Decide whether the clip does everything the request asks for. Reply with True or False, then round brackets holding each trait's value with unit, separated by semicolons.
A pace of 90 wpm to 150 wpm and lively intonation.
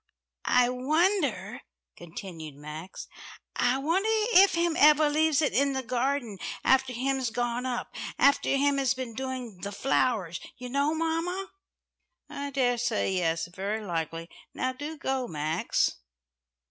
True (135 wpm; 5.8 semitones)